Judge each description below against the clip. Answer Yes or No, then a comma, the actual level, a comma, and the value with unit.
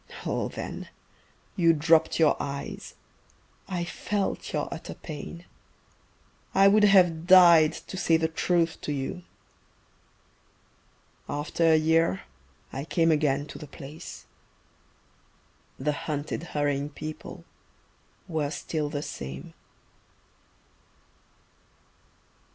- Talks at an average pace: No, slow, 100 wpm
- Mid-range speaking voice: Yes, medium, 160 Hz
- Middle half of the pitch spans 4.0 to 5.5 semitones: No, average, 2.7 semitones